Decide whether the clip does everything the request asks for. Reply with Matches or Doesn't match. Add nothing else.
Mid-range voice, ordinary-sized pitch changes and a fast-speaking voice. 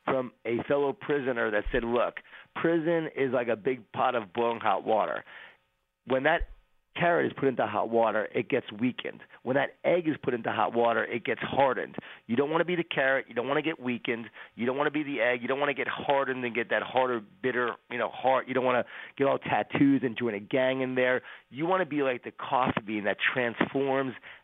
Doesn't match